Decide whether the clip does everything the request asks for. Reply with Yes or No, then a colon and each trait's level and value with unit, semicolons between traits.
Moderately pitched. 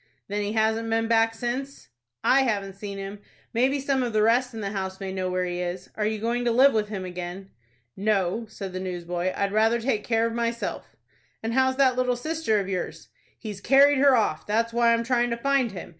No: high, 225 Hz